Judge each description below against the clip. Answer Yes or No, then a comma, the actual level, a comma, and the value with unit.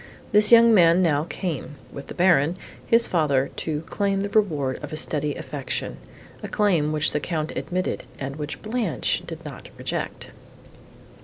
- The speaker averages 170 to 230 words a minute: No, average, 160 wpm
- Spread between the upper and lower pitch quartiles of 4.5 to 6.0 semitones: Yes, average, 5.2 semitones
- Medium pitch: Yes, medium, 165 Hz